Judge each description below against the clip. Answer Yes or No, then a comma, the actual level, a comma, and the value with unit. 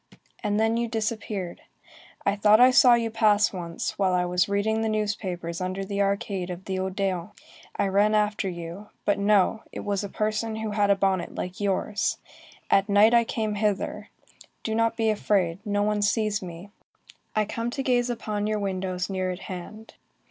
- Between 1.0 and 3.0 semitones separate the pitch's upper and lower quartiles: Yes, narrow, 2.4 semitones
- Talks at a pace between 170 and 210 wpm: Yes, average, 185 wpm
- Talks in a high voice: Yes, high, 205 Hz